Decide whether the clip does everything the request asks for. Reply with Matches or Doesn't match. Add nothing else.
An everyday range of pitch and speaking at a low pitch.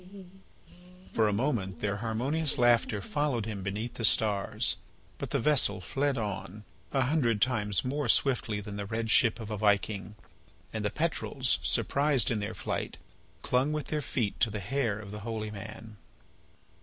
Matches